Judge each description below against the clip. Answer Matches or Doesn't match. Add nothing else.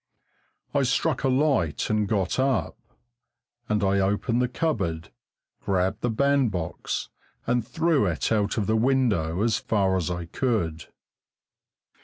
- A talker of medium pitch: Doesn't match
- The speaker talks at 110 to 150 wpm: Matches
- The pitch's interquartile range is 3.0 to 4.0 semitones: Doesn't match